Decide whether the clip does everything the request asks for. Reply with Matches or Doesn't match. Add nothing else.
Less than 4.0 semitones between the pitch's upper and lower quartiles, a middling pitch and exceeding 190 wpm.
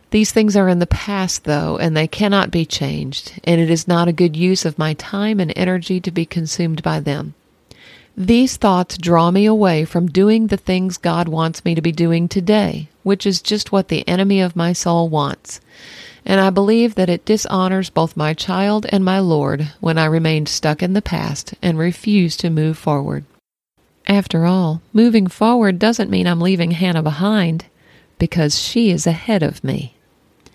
Doesn't match